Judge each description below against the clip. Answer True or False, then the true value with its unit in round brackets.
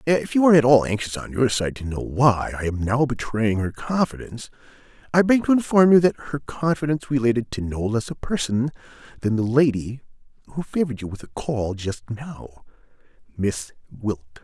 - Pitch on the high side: False (125 Hz)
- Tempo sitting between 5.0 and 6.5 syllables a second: True (5.4 syllables/s)